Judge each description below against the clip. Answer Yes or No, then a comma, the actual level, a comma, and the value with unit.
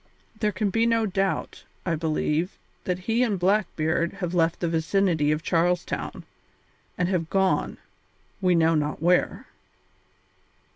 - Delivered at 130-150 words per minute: Yes, average, 140 wpm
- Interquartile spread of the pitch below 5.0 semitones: Yes, average, 3.0 semitones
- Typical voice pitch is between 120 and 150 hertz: No, medium, 180 Hz